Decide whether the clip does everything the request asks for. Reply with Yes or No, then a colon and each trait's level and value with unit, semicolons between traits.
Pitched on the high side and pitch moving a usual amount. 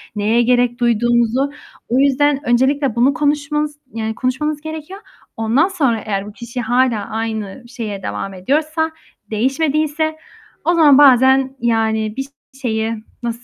Yes: very high, 250 Hz; average, 4.5 semitones